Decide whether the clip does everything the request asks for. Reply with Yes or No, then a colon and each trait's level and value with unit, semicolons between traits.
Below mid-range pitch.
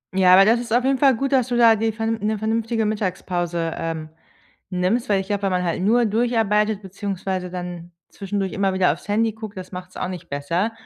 No: high, 200 Hz